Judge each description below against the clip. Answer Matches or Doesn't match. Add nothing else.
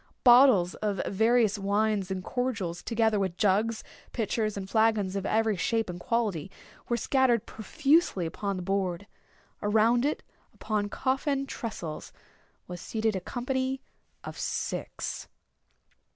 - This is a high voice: Matches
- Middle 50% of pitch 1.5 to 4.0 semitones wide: Matches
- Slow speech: Matches